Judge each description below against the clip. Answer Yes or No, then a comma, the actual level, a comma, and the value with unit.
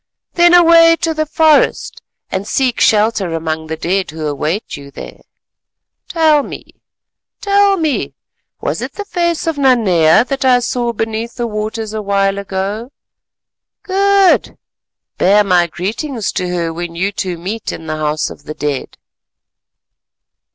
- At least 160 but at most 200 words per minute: No, average, 145 wpm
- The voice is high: Yes, high, 215 Hz